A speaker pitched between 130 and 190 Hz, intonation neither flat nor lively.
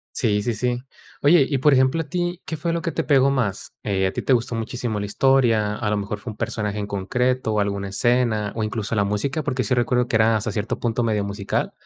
No: low, 115 Hz; average, 4.1 semitones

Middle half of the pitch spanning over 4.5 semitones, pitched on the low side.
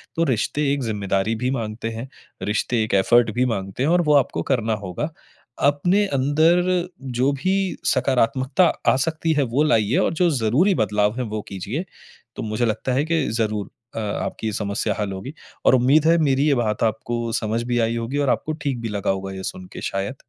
Yes: average, 5.0 semitones; low, 120 Hz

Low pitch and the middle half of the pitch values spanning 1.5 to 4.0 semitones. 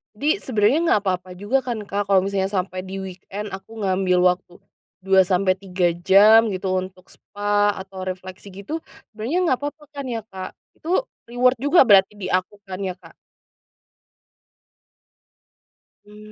No: high, 195 Hz; average, 2.9 semitones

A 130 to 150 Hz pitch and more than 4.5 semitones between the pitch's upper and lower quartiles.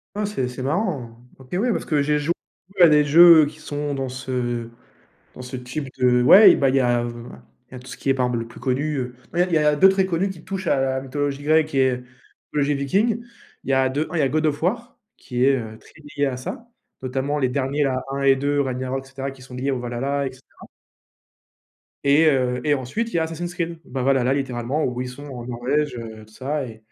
No: low, 135 Hz; average, 3.1 semitones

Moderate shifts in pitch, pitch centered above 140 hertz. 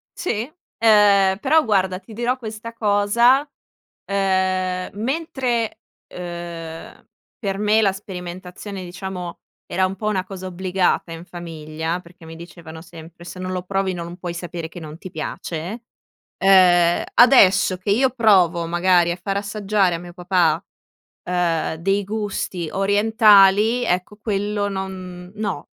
Yes: average, 3.0 semitones; high, 190 Hz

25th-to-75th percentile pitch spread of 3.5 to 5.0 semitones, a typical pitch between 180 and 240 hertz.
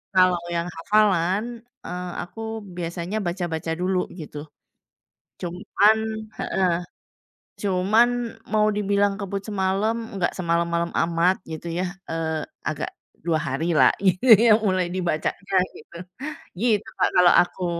No: average, 3.1 semitones; medium, 185 Hz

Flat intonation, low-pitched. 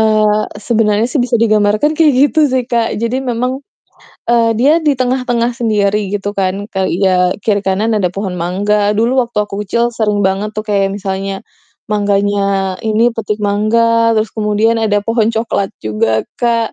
No: narrow, 2.3 semitones; high, 215 Hz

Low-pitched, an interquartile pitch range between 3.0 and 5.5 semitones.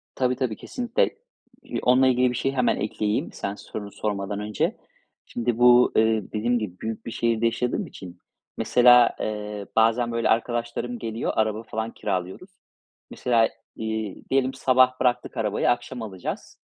No: low, 115 Hz; narrow, 2.5 semitones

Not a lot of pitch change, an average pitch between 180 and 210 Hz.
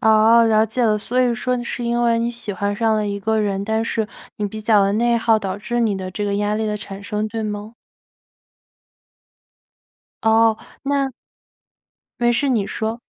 No: narrow, 2.1 semitones; high, 220 Hz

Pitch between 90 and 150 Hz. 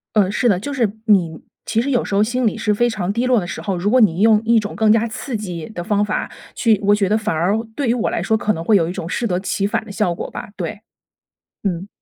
No: high, 210 Hz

